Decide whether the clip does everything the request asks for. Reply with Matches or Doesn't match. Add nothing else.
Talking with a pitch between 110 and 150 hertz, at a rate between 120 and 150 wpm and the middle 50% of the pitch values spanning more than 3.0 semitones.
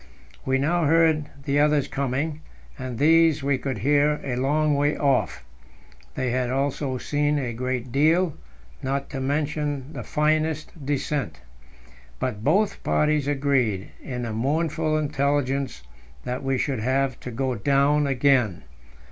Doesn't match